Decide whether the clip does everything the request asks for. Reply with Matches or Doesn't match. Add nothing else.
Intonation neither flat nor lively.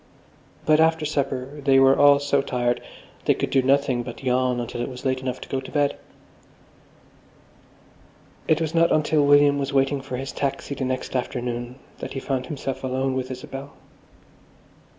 Doesn't match